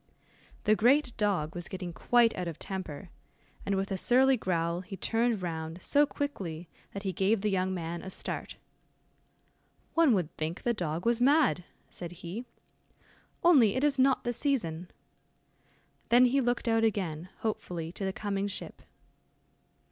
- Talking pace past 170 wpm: No, average, 155 wpm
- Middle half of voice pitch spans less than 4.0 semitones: No, wide, 5.6 semitones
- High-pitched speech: Yes, high, 195 Hz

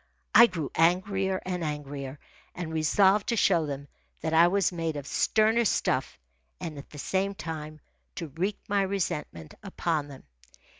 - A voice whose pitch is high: No, medium, 165 Hz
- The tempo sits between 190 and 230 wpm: No, average, 155 wpm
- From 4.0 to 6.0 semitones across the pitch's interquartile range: Yes, average, 4.4 semitones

